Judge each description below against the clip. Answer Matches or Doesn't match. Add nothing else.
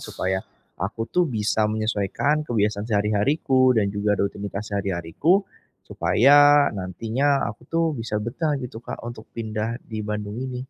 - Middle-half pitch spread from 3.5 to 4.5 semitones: Matches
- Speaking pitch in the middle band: Doesn't match